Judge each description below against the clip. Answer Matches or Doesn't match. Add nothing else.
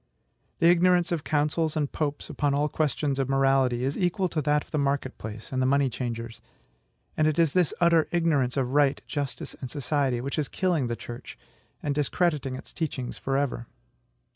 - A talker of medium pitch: Matches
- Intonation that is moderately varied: Matches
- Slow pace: Doesn't match